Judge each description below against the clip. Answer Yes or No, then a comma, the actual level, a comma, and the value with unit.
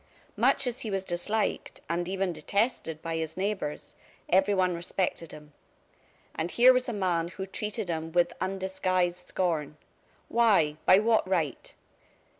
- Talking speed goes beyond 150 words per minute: No, average, 140 wpm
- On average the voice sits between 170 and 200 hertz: Yes, medium, 185 Hz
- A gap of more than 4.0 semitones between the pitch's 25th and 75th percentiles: No, average, 3.3 semitones